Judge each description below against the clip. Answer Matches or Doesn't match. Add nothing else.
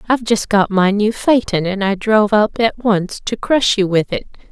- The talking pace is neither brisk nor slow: Doesn't match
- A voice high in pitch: Matches